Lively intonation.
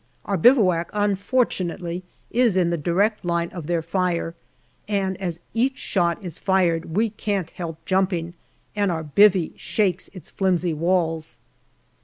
No: average, 2.9 semitones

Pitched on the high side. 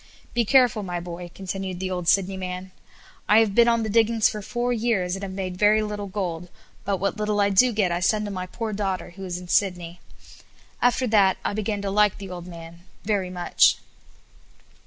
Yes: high, 195 Hz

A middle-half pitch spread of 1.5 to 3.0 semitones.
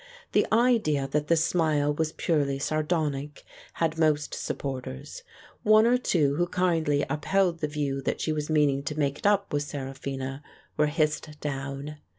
Yes: narrow, 2.6 semitones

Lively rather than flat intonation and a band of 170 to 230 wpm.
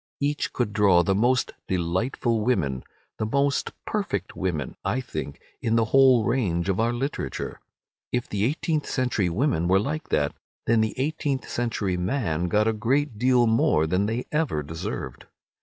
No: wide, 6.0 semitones; average, 155 wpm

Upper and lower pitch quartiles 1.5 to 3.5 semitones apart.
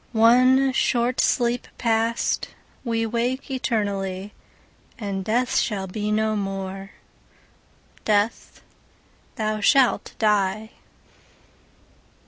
Yes: average, 2.9 semitones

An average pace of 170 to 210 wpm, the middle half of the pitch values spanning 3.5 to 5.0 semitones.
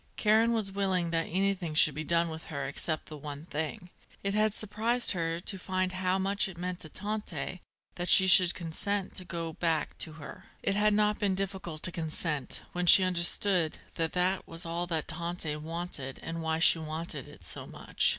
No: average, 195 wpm; average, 3.1 semitones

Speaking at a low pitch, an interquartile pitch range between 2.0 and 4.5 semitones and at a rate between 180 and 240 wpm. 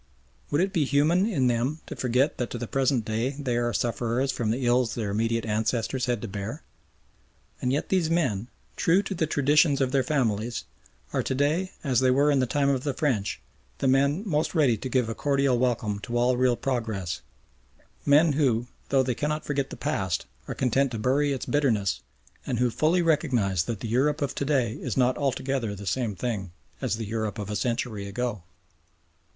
Yes: low, 130 Hz; average, 3.8 semitones; average, 200 wpm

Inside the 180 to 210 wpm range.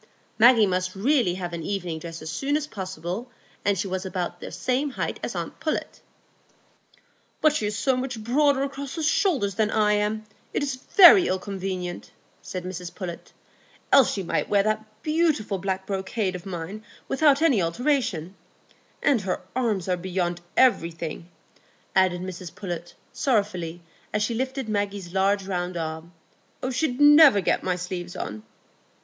No: average, 155 wpm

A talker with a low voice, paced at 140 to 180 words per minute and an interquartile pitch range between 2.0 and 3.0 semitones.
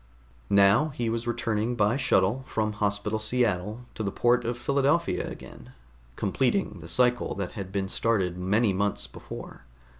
No: low, 110 Hz; average, 150 wpm; average, 3.4 semitones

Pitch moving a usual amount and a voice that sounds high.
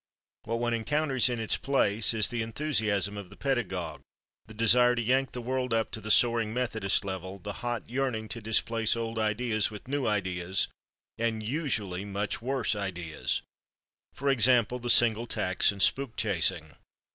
No: average, 3.2 semitones; low, 115 Hz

